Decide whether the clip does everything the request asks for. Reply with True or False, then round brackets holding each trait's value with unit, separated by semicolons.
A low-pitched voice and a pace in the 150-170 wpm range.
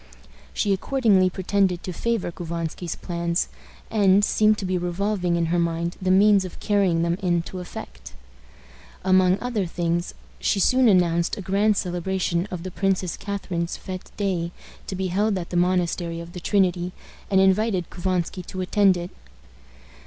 False (185 Hz; 155 wpm)